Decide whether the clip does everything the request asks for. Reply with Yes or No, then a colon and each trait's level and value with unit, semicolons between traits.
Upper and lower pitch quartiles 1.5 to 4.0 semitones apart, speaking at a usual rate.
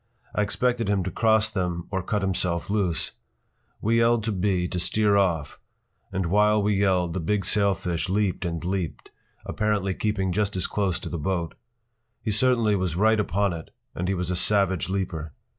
Yes: average, 2.8 semitones; average, 180 wpm